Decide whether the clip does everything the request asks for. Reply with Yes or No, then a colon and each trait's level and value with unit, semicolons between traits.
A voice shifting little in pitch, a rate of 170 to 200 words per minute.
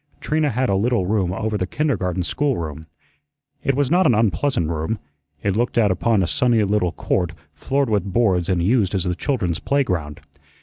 No: wide, 5.6 semitones; average, 180 wpm